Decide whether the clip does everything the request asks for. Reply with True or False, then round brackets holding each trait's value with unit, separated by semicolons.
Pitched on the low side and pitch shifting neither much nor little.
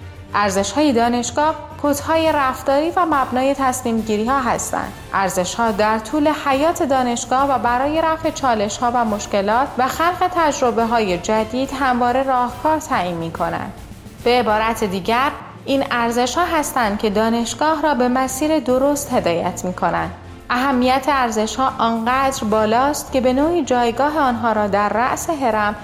False (250 Hz; 4.4 semitones)